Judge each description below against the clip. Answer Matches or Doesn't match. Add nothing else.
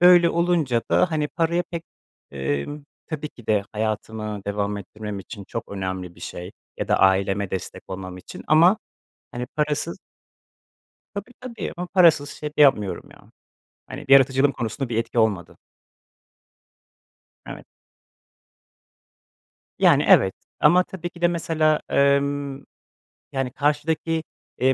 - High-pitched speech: Doesn't match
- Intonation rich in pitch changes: Matches